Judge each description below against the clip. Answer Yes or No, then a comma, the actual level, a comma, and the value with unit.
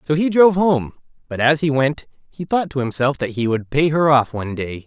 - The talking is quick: Yes, fast, 245 wpm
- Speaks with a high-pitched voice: No, medium, 140 Hz